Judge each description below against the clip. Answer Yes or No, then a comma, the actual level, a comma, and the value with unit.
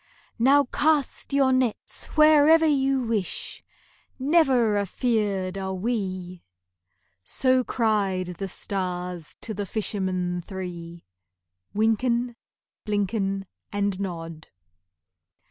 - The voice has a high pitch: Yes, high, 205 Hz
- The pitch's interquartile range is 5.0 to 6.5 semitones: Yes, wide, 5.5 semitones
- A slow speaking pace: Yes, slow, 90 wpm